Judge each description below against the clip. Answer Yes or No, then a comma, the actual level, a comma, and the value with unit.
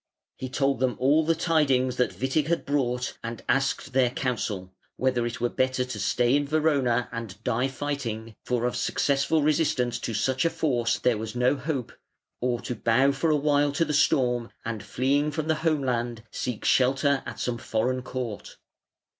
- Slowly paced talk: No, average, 180 wpm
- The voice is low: Yes, low, 130 Hz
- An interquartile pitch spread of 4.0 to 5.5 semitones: No, average, 3.1 semitones